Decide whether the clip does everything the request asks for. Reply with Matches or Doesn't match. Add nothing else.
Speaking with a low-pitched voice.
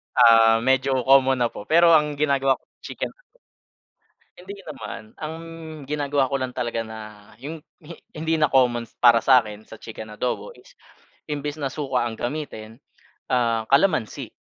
Matches